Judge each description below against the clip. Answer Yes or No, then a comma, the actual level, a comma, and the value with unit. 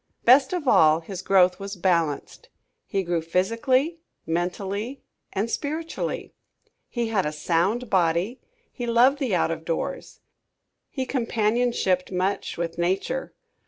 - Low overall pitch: No, high, 195 Hz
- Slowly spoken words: Yes, slow, 125 wpm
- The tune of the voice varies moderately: No, wide, 6.0 semitones